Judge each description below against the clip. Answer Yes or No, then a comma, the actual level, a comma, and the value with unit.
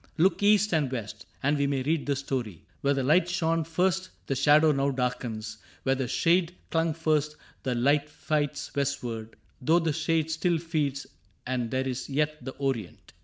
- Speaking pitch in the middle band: Yes, medium, 145 Hz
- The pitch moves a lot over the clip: No, average, 3.7 semitones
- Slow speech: No, average, 180 wpm